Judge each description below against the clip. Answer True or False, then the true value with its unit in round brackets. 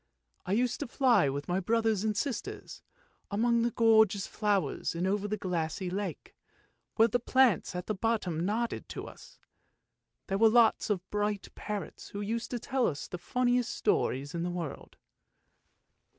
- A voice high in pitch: True (210 Hz)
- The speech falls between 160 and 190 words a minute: True (165 wpm)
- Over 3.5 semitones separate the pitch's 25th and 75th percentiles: True (4.1 semitones)